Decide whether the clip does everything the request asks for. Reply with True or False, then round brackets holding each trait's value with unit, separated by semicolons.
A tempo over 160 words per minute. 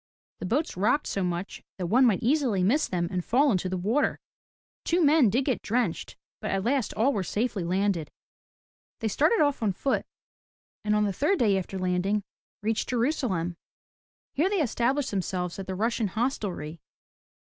True (170 wpm)